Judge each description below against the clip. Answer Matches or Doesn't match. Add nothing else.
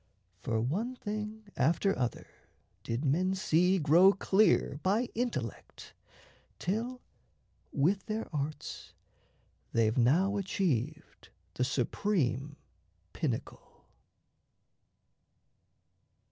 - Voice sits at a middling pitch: Matches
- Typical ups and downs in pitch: Doesn't match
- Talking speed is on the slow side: Matches